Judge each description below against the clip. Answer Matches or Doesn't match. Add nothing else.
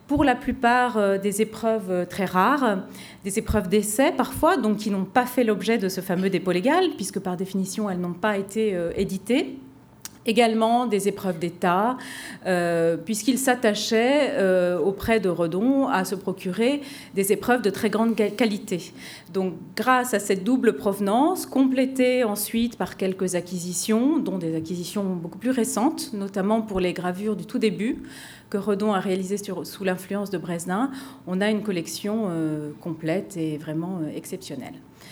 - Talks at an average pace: Matches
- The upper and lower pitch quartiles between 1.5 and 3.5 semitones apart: Doesn't match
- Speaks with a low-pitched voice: Doesn't match